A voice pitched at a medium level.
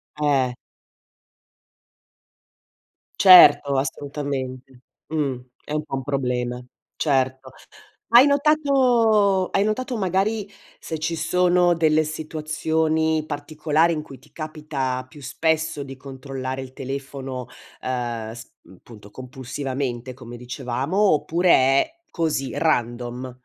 Yes: medium, 145 Hz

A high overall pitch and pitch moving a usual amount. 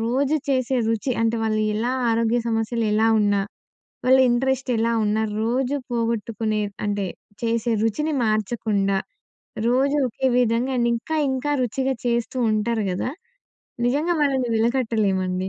Yes: high, 230 Hz; average, 3.0 semitones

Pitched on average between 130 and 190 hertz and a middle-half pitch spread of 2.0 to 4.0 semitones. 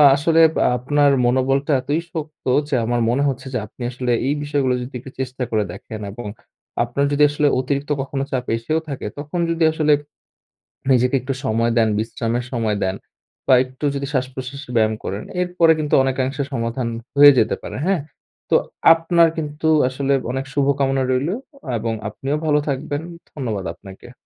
Yes: low, 135 Hz; average, 3.1 semitones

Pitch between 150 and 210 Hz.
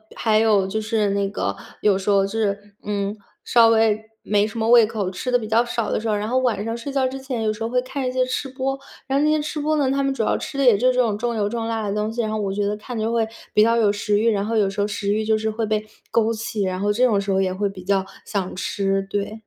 No: high, 220 Hz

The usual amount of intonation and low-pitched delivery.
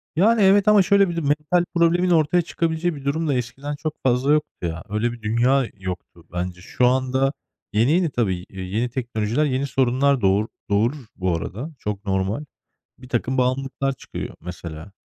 No: wide, 6.3 semitones; low, 130 Hz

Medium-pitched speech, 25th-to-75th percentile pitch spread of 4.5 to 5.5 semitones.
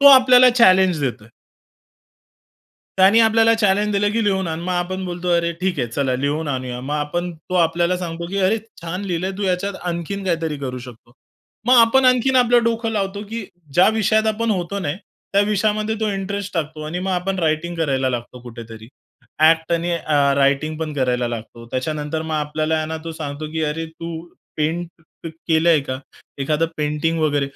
Yes: medium, 170 Hz; average, 4.8 semitones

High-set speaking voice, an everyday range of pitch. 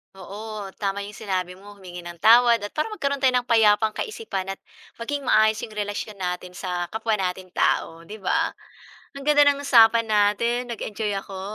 Yes: high, 210 Hz; average, 3.7 semitones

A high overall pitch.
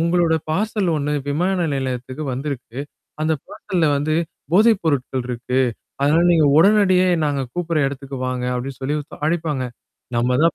No: medium, 150 Hz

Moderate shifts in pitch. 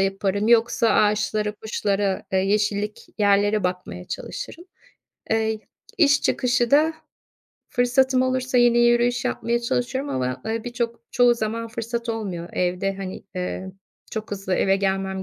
Yes: average, 3.6 semitones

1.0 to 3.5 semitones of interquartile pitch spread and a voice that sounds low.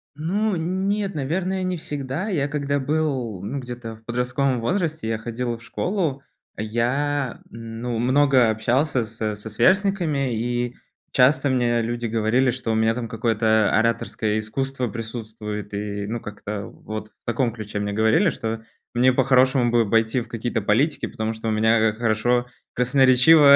No: average, 3.9 semitones; low, 120 Hz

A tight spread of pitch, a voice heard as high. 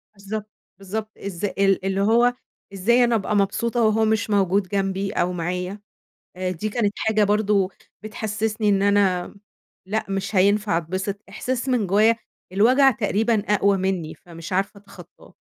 Yes: narrow, 2.2 semitones; high, 200 Hz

